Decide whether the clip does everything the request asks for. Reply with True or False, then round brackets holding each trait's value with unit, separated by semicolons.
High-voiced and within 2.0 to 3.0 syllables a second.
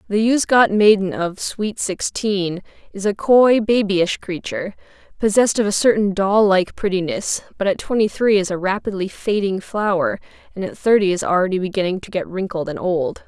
False (195 Hz; 5.1 syllables/s)